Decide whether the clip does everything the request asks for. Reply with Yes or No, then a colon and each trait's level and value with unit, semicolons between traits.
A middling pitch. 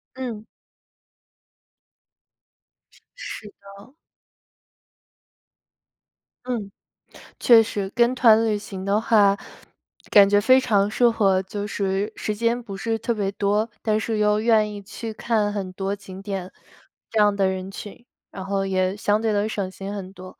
No: high, 205 Hz